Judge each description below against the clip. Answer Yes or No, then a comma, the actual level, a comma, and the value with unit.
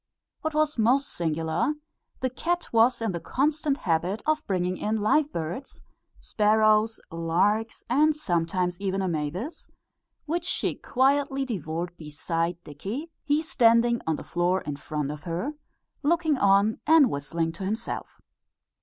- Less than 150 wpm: Yes, average, 140 wpm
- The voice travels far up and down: Yes, wide, 8.4 semitones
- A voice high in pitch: Yes, high, 215 Hz